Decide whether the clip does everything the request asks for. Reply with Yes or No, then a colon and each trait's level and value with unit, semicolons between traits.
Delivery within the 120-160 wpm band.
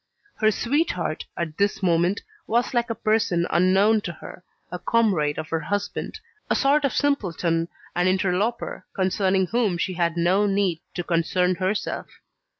Yes: average, 150 wpm